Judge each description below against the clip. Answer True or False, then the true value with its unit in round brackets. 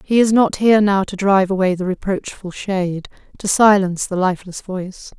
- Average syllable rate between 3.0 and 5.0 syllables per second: False (5.7 syllables/s)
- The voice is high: True (195 Hz)